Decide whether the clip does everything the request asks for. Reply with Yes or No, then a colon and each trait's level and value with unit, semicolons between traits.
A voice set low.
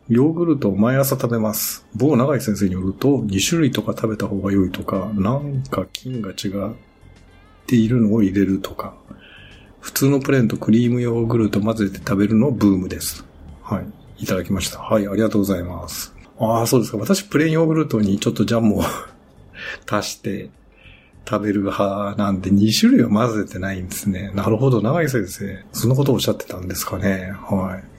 Yes: low, 105 Hz